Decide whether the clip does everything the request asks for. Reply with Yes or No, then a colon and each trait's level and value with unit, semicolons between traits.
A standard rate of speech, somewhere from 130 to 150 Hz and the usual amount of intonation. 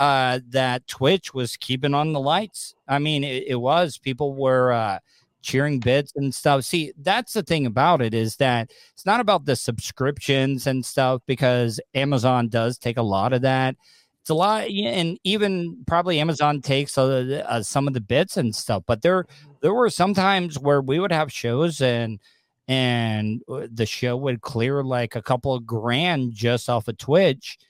Yes: average, 180 wpm; low, 135 Hz; average, 3.7 semitones